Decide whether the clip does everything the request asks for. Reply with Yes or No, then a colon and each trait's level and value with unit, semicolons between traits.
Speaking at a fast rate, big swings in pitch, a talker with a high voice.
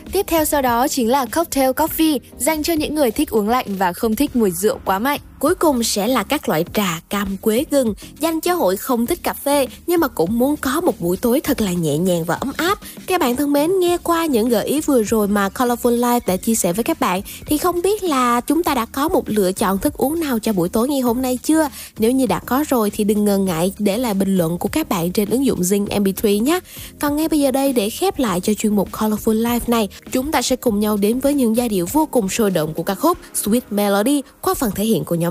Yes: fast, 265 wpm; wide, 5.8 semitones; high, 245 Hz